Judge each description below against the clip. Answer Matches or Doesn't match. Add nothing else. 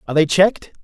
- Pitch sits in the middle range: Matches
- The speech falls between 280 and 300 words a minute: Doesn't match